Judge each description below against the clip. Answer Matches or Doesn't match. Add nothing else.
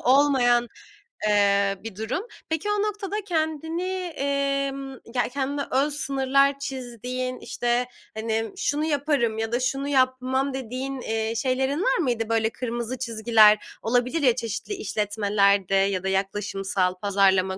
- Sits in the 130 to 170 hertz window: Doesn't match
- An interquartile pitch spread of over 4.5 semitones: Doesn't match